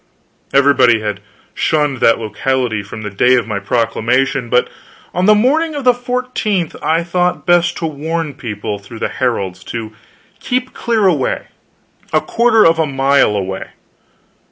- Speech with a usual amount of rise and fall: No, wide, 7.8 semitones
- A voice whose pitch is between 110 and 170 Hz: Yes, medium, 140 Hz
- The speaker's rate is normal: Yes, average, 155 wpm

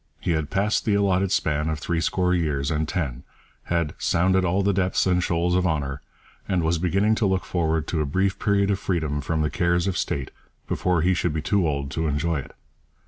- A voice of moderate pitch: No, very low, 85 Hz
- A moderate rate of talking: No, fast, 210 wpm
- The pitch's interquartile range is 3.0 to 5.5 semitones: Yes, average, 3.4 semitones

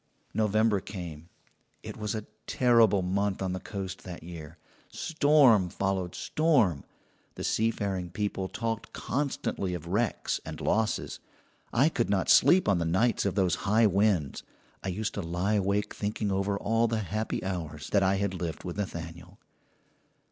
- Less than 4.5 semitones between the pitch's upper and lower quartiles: Yes, average, 3.3 semitones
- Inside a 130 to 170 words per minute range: Yes, average, 155 wpm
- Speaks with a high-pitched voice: No, low, 100 Hz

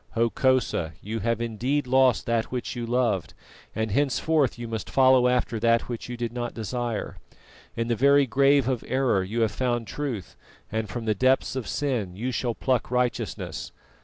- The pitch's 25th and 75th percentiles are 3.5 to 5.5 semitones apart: No, narrow, 2.5 semitones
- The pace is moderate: Yes, average, 175 wpm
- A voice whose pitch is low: Yes, low, 120 Hz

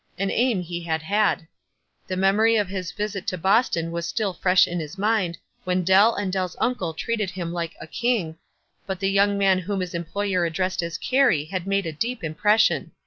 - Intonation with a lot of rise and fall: No, average, 3.2 semitones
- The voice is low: No, high, 190 Hz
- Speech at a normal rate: Yes, average, 195 wpm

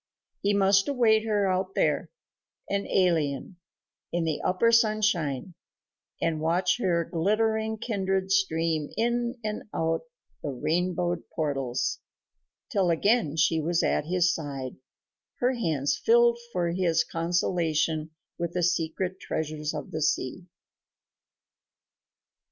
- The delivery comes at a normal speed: No, slow, 115 wpm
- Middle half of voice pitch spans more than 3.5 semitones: Yes, average, 4.2 semitones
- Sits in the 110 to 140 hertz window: No, medium, 175 Hz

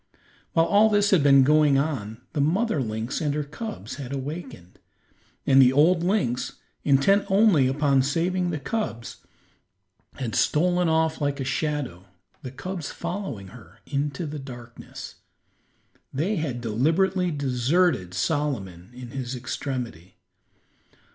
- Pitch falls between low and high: Yes, medium, 145 Hz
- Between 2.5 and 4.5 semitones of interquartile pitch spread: No, average, 5.0 semitones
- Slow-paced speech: Yes, slow, 130 wpm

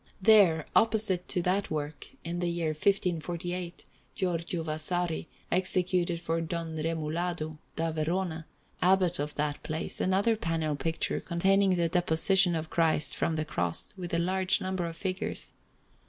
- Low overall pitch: No, medium, 170 Hz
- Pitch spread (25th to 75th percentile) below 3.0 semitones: Yes, narrow, 2.4 semitones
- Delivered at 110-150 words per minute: Yes, average, 140 wpm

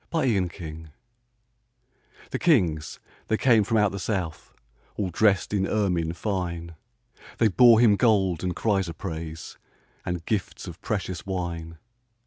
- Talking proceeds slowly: Yes, slow, 125 wpm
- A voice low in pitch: Yes, very low, 95 Hz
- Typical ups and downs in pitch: Yes, average, 4.1 semitones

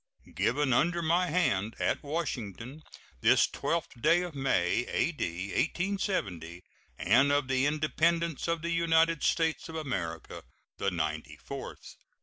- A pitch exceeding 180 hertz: No, medium, 145 Hz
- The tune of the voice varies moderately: No, wide, 8.8 semitones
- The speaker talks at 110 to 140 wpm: Yes, slow, 135 wpm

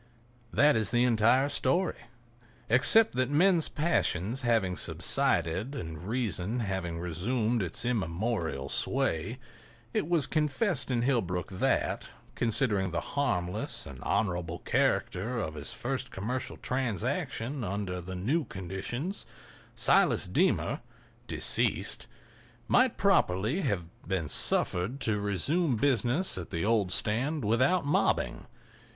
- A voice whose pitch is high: No, low, 115 Hz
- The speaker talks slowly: Yes, slow, 115 wpm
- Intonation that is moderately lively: No, wide, 6.1 semitones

